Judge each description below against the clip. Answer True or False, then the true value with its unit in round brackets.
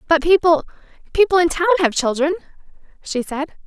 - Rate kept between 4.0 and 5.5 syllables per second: False (5.7 syllables/s)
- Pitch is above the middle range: True (325 Hz)